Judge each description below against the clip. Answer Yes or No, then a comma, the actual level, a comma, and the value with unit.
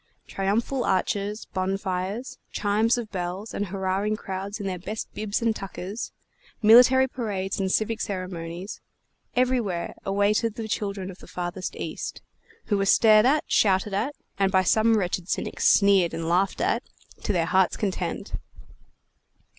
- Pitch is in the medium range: No, high, 200 Hz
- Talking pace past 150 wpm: No, average, 145 wpm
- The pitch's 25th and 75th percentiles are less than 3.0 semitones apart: Yes, narrow, 2.6 semitones